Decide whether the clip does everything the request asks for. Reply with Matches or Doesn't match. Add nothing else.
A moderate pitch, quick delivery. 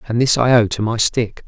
Doesn't match